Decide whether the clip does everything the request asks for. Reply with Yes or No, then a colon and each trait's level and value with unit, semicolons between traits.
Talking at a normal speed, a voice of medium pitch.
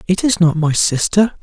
No: fast, 210 wpm; medium, 180 Hz